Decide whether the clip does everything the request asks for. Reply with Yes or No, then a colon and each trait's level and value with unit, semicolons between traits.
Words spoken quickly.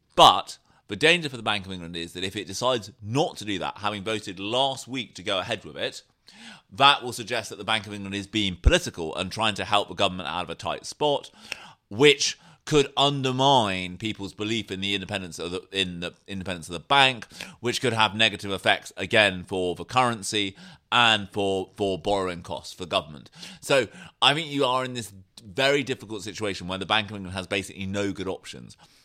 Yes: fast, 210 wpm